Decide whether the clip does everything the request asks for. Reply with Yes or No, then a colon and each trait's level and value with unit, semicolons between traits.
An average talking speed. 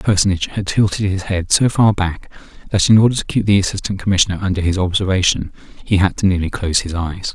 No: fast, 220 wpm